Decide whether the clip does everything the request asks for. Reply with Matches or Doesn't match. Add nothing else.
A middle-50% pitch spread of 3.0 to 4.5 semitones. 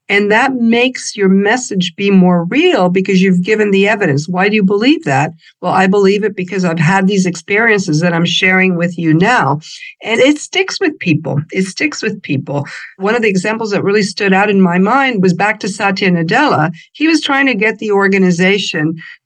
Matches